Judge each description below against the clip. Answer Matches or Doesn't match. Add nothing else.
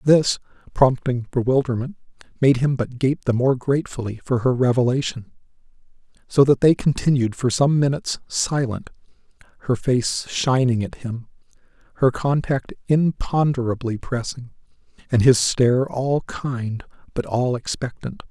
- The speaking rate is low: Matches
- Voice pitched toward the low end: Matches